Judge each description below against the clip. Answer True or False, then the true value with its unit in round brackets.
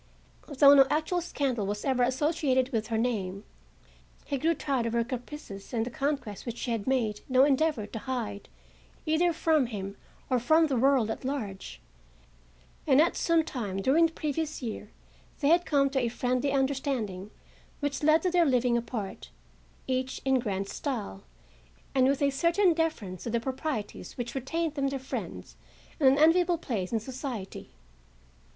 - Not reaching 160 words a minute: False (165 wpm)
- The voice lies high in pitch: True (260 Hz)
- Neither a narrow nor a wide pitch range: True (4.5 semitones)